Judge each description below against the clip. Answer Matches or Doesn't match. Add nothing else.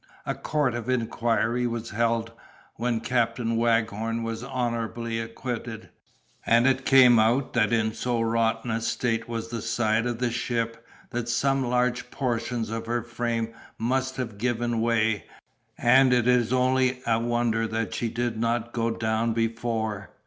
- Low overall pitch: Matches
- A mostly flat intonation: Matches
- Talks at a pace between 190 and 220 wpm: Doesn't match